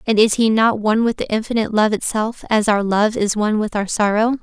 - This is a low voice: No, high, 215 Hz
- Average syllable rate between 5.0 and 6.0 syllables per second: Yes, 5.9 syllables/s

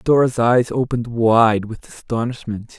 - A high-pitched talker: No, low, 115 Hz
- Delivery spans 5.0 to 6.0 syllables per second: No, 4.5 syllables/s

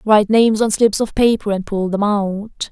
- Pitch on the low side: No, high, 210 Hz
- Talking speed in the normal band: No, fast, 220 wpm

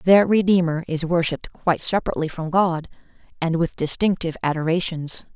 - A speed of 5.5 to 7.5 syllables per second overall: Yes, 5.8 syllables/s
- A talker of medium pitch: Yes, medium, 170 Hz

